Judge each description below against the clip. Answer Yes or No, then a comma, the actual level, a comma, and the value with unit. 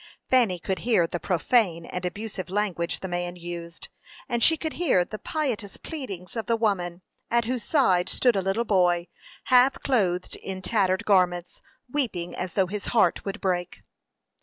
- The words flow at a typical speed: Yes, average, 165 wpm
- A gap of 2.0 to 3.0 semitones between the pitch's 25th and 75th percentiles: No, average, 4.8 semitones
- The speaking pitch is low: No, high, 195 Hz